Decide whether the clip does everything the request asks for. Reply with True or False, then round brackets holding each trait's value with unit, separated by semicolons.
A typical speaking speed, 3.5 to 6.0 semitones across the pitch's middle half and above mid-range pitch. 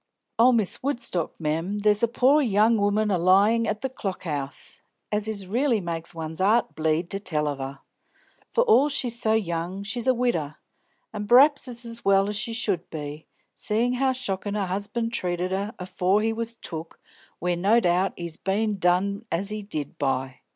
True (185 wpm; 4.9 semitones; 200 Hz)